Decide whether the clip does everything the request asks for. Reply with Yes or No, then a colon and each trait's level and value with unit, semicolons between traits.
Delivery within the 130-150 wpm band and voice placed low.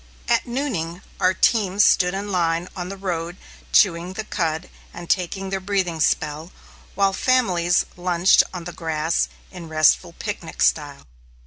No: average, 145 wpm; medium, 180 Hz